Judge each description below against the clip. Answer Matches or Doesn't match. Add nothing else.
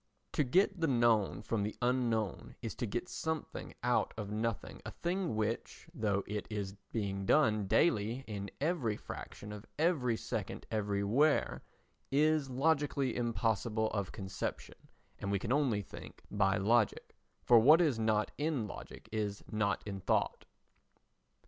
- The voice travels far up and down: Doesn't match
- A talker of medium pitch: Doesn't match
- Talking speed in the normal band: Matches